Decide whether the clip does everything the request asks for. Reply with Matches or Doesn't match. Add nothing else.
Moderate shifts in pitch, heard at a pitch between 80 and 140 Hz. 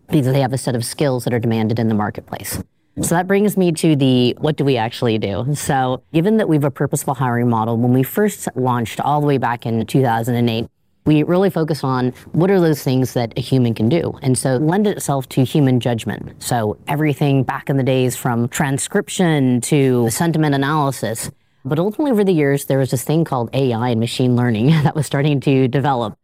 Matches